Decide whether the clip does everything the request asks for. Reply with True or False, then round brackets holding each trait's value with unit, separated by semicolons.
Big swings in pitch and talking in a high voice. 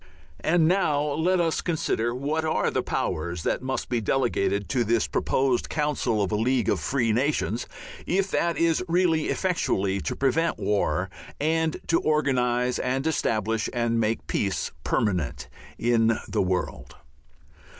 False (6.1 semitones; 130 Hz)